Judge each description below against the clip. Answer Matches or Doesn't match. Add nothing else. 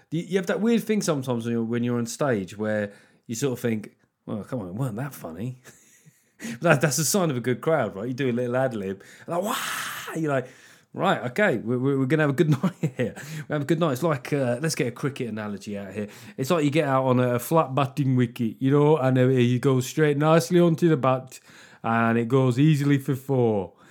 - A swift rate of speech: Matches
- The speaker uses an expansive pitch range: Doesn't match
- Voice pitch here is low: Matches